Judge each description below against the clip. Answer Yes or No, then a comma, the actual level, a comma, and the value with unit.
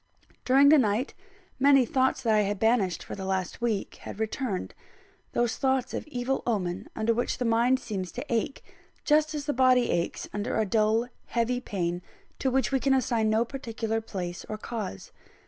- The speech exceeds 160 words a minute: Yes, average, 180 wpm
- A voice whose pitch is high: Yes, high, 230 Hz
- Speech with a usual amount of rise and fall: Yes, average, 3.7 semitones